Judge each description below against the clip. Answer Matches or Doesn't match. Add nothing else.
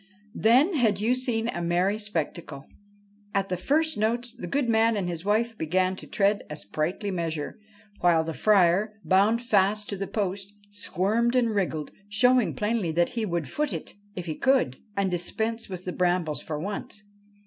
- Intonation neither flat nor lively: Matches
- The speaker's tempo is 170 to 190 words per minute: Matches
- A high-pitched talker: Matches